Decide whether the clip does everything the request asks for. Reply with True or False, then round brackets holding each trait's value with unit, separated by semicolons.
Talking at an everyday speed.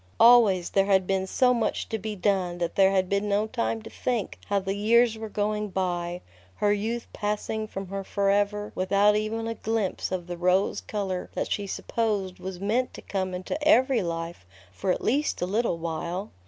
True (195 wpm)